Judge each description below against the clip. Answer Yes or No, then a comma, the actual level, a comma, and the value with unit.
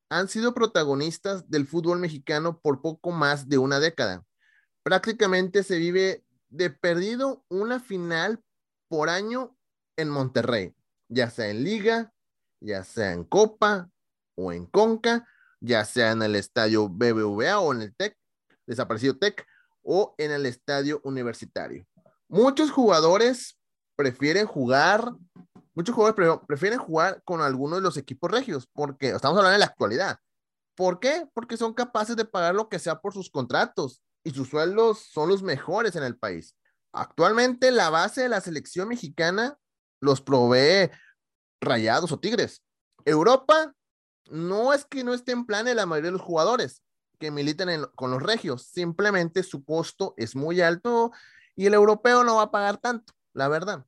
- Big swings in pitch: Yes, wide, 7.9 semitones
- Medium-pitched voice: Yes, medium, 175 Hz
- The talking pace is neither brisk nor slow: Yes, average, 155 wpm